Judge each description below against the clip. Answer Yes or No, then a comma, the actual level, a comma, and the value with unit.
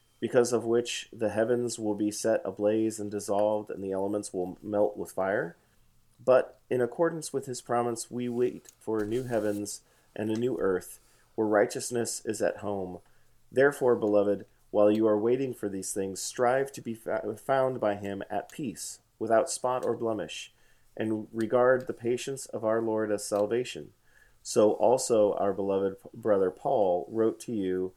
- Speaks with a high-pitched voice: No, low, 110 Hz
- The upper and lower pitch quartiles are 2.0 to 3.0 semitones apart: Yes, average, 2.7 semitones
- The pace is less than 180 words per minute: Yes, average, 165 wpm